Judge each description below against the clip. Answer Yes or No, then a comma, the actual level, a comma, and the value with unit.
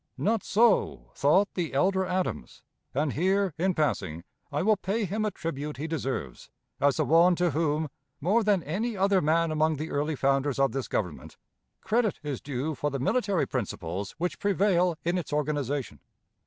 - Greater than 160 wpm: Yes, average, 170 wpm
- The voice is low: No, medium, 160 Hz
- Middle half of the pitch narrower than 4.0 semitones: No, average, 5.3 semitones